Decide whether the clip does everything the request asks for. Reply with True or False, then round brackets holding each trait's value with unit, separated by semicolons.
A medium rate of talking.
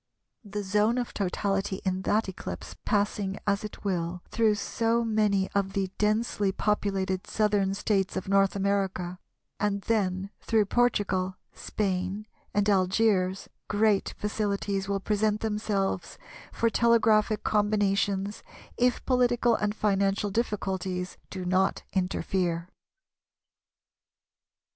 False (110 wpm)